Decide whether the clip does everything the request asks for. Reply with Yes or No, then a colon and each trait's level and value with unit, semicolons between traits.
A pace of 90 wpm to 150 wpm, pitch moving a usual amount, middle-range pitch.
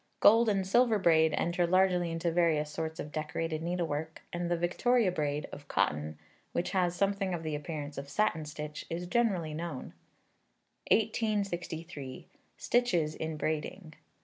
Yes: average, 145 wpm; average, 3.6 semitones; medium, 170 Hz